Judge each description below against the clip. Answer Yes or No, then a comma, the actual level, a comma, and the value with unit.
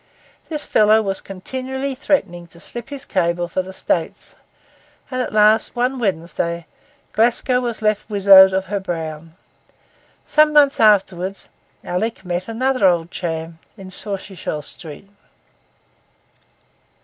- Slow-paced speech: Yes, slow, 125 wpm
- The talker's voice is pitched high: Yes, high, 195 Hz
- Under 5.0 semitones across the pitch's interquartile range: No, wide, 5.4 semitones